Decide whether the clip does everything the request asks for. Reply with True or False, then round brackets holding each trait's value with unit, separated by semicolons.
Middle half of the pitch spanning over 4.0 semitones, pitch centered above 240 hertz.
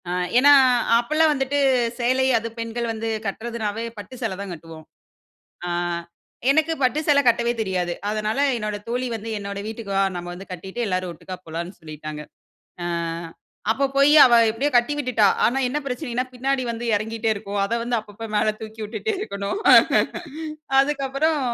False (4.4 semitones; 225 Hz)